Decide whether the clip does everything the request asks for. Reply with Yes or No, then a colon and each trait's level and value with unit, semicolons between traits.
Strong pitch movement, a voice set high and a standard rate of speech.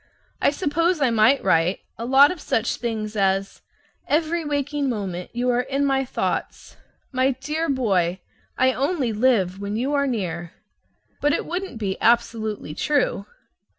Yes: wide, 5.7 semitones; very high, 250 Hz; average, 150 wpm